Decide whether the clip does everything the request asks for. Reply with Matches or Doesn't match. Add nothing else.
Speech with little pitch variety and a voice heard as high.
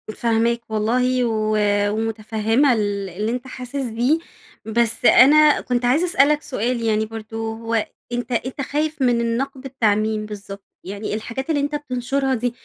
Doesn't match